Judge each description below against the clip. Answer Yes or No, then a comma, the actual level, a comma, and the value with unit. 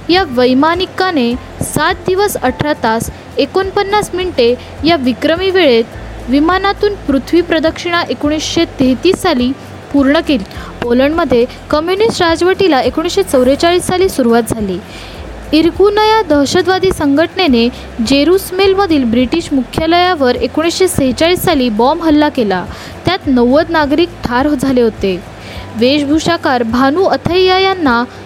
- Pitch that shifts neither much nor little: No, wide, 6.1 semitones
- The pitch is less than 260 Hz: No, very high, 310 Hz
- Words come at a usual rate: Yes, average, 100 wpm